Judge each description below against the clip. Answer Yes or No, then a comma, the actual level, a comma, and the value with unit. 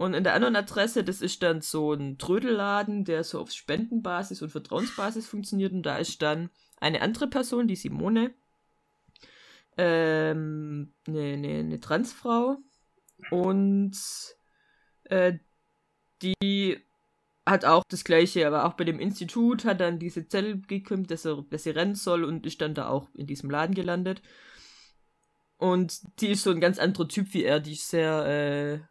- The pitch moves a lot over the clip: No, average, 4.4 semitones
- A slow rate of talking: No, average, 160 wpm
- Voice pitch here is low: No, medium, 180 Hz